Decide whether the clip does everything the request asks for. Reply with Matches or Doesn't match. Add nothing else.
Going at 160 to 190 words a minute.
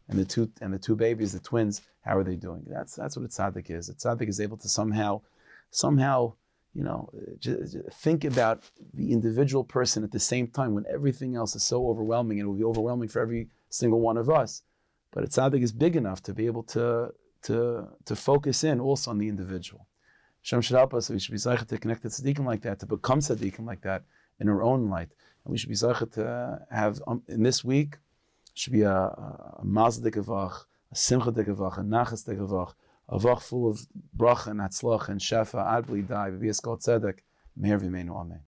Doesn't match